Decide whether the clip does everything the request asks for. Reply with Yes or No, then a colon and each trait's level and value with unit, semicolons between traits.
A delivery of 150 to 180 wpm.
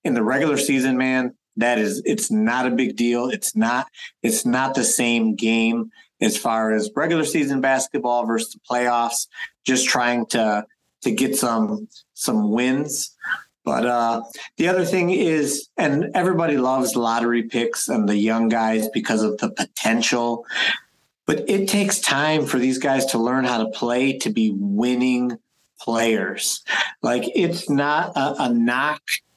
Yes: average, 155 wpm